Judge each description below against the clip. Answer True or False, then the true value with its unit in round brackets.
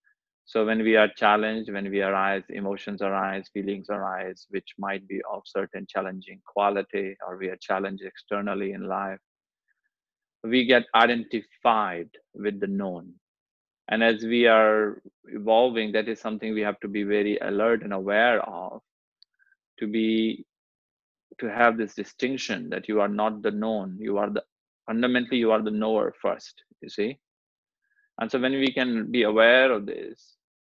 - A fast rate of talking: False (160 wpm)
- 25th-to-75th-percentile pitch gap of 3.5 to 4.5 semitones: False (2.6 semitones)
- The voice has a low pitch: True (110 Hz)